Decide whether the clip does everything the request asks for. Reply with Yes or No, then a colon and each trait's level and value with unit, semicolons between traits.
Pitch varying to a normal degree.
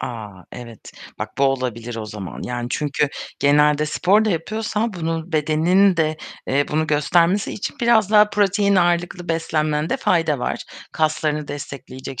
Yes: average, 4.3 semitones